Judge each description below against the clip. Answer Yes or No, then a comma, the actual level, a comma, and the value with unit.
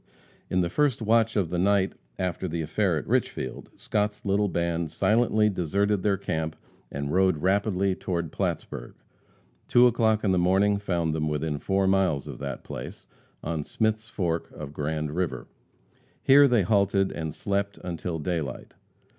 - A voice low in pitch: Yes, very low, 95 Hz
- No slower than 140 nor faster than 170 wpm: Yes, average, 160 wpm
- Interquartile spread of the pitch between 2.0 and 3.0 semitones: No, average, 4.1 semitones